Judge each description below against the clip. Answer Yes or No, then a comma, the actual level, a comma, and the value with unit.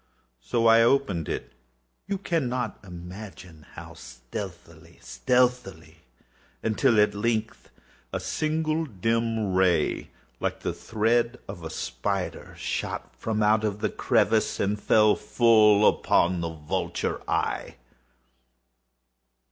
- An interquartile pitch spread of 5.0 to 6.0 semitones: Yes, average, 5.3 semitones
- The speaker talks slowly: Yes, slow, 100 wpm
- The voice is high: No, low, 105 Hz